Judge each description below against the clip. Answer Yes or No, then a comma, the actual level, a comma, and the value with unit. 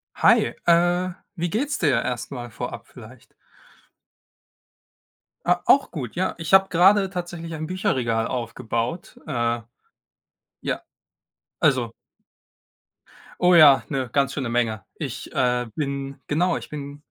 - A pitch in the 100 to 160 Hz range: Yes, medium, 140 Hz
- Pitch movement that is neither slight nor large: No, wide, 6.1 semitones